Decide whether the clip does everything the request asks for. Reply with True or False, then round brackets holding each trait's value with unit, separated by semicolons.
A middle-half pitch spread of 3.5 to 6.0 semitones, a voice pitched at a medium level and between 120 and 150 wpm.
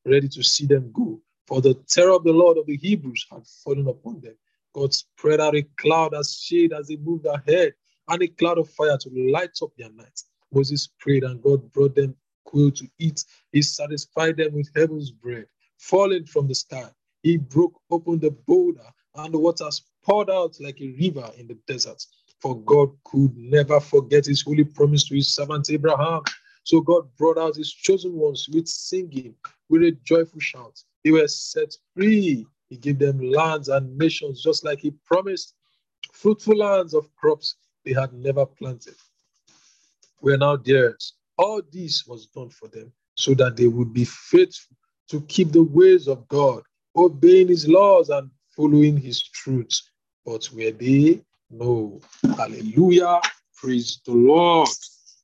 False (3.9 semitones; 150 Hz; 170 wpm)